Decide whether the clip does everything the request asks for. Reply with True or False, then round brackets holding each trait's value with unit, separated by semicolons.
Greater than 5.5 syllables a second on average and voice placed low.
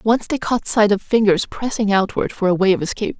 False (5.7 syllables/s; 210 Hz)